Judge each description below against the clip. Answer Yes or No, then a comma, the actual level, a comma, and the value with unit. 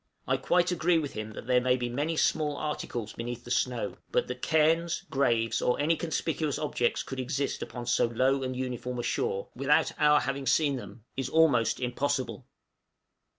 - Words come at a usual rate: Yes, average, 180 wpm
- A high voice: No, low, 135 Hz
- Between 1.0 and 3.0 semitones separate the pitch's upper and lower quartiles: No, average, 4.0 semitones